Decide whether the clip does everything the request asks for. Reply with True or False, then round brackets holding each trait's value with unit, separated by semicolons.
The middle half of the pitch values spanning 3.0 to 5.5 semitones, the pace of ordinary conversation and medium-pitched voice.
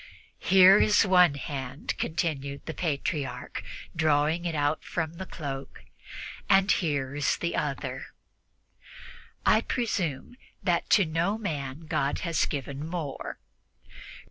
False (4.0 semitones; 115 wpm; 155 Hz)